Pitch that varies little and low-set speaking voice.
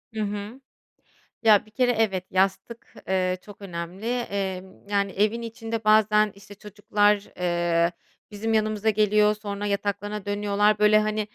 No: narrow, 1.4 semitones; high, 205 Hz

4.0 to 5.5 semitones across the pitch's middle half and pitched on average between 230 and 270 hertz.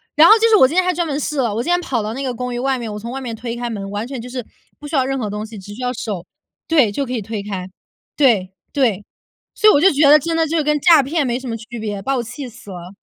Yes: average, 5.1 semitones; very high, 250 Hz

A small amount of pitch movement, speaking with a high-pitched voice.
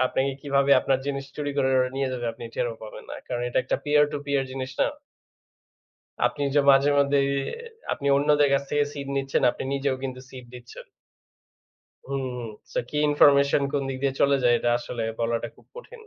No: narrow, 1.8 semitones; low, 135 Hz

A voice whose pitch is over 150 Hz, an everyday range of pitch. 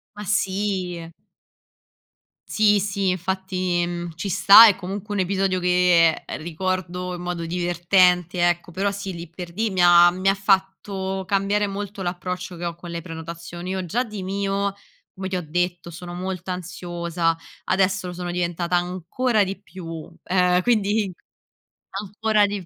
No: medium, 185 Hz; narrow, 2.0 semitones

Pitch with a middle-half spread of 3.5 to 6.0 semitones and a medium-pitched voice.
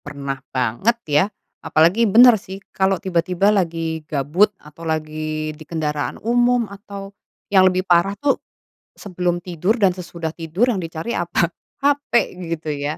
Yes: average, 4.3 semitones; medium, 175 Hz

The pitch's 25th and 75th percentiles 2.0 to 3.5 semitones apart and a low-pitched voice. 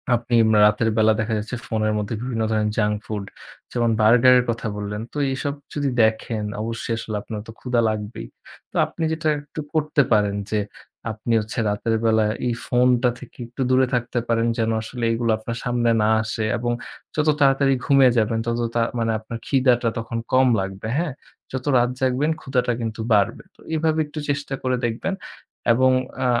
Yes: average, 2.8 semitones; low, 115 Hz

